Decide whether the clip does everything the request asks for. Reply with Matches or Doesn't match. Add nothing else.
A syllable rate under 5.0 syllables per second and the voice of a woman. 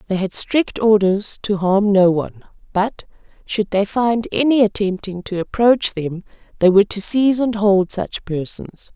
Matches